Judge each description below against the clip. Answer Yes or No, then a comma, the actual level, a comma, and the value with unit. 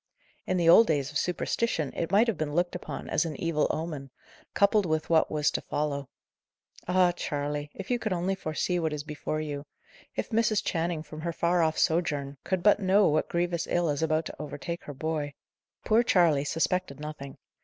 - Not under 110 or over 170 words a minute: No, average, 195 wpm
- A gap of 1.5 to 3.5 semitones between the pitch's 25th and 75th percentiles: Yes, average, 3.2 semitones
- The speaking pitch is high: No, medium, 160 Hz